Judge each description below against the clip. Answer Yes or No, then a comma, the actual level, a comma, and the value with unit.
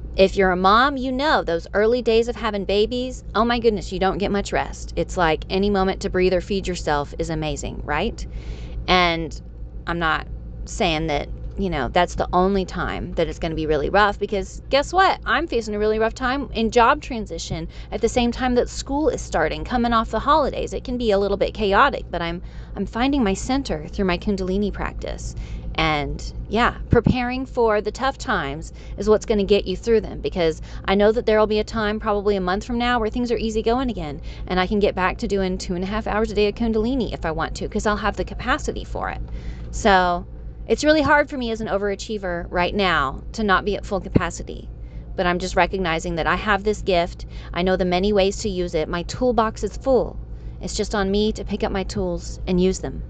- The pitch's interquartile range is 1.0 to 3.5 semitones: No, average, 4.2 semitones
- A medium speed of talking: No, fast, 230 wpm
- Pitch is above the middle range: Yes, high, 195 Hz